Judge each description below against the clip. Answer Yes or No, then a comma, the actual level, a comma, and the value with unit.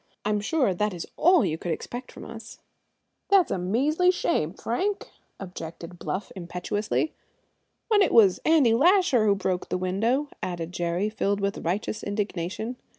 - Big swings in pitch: Yes, wide, 6.7 semitones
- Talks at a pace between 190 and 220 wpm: No, average, 150 wpm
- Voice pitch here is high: Yes, high, 210 Hz